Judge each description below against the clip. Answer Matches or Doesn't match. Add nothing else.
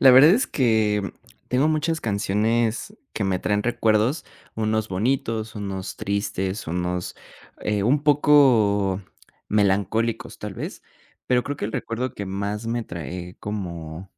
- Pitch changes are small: Doesn't match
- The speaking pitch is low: Matches